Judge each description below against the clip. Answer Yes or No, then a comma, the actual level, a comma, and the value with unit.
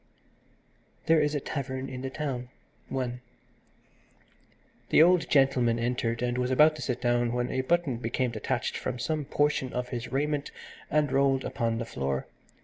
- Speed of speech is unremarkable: Yes, average, 160 wpm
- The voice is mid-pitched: No, low, 130 Hz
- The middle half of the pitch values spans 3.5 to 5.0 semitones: No, average, 3.1 semitones